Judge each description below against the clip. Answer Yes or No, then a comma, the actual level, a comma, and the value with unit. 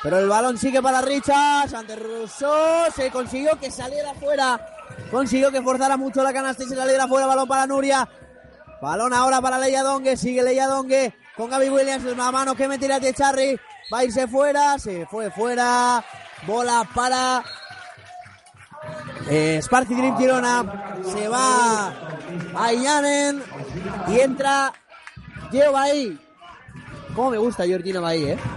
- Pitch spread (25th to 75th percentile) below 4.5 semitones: Yes, average, 2.9 semitones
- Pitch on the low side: No, very high, 260 Hz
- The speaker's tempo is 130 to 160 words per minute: Yes, average, 145 wpm